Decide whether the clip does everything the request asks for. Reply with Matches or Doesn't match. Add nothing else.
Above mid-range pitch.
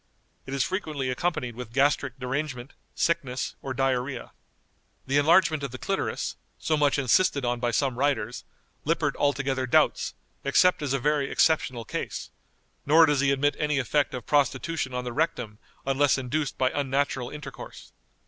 Doesn't match